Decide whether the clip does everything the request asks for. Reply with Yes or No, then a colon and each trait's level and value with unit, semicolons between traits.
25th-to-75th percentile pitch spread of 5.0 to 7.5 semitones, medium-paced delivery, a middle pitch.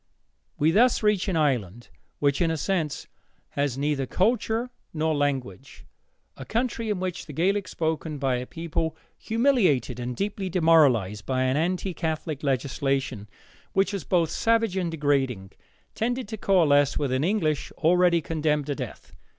Yes: wide, 5.6 semitones; average, 150 wpm; medium, 160 Hz